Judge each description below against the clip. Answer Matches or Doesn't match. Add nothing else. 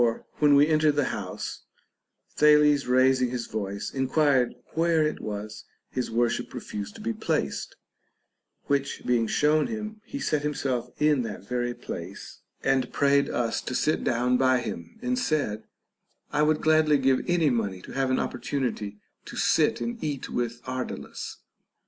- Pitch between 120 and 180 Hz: Matches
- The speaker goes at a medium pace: Matches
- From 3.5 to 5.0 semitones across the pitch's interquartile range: Matches